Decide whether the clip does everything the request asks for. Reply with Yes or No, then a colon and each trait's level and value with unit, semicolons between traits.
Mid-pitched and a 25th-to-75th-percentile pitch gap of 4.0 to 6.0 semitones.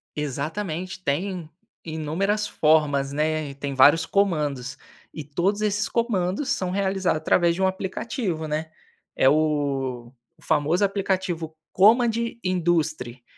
Yes: medium, 165 Hz; average, 4.4 semitones